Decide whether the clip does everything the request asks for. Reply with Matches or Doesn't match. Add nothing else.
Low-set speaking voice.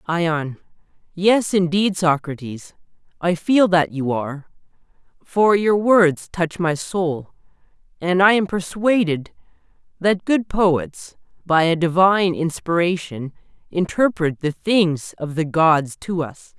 Doesn't match